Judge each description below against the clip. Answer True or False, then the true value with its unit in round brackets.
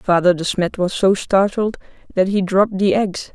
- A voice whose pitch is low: False (190 Hz)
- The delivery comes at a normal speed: True (195 wpm)